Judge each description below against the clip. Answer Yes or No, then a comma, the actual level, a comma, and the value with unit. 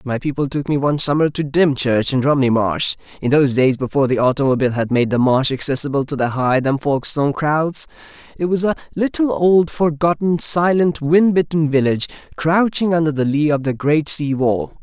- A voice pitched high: No, medium, 145 Hz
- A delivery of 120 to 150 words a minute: No, average, 190 wpm